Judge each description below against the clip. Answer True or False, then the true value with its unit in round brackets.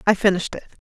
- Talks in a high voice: True (195 Hz)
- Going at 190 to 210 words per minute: True (205 wpm)